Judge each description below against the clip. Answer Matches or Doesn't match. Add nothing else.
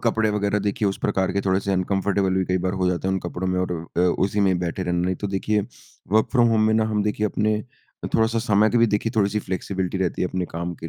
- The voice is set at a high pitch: Doesn't match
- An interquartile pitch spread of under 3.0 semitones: Matches